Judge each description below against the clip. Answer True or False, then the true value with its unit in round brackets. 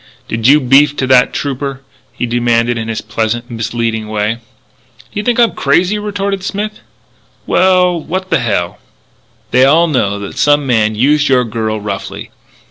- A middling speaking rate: True (165 wpm)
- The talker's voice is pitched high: False (125 Hz)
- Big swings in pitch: True (6.7 semitones)